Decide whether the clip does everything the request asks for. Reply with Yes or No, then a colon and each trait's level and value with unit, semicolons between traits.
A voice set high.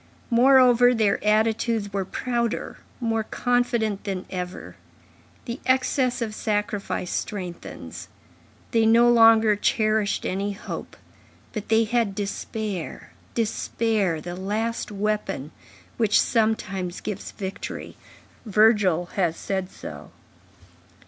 Yes: high, 215 Hz